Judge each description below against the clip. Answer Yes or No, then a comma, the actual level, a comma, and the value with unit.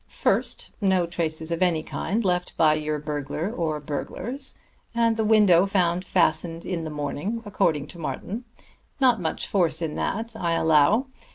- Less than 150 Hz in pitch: No, medium, 175 Hz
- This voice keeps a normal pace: Yes, average, 160 wpm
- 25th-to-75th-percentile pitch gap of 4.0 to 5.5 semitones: Yes, average, 4.6 semitones